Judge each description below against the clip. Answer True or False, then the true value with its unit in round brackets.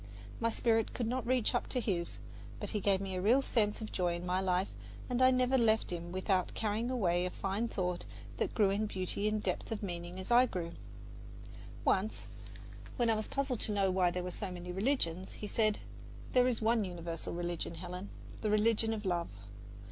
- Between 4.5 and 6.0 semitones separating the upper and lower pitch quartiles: False (3.9 semitones)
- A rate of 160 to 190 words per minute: False (200 wpm)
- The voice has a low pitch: False (200 Hz)